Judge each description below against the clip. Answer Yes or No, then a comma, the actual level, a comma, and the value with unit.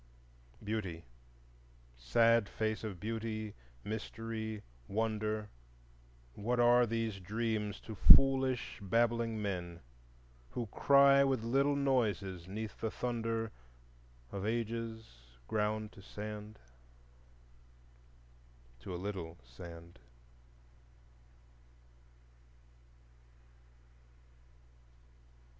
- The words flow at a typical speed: No, slow, 75 wpm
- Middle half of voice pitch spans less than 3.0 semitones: Yes, narrow, 2.6 semitones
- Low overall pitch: Yes, low, 110 Hz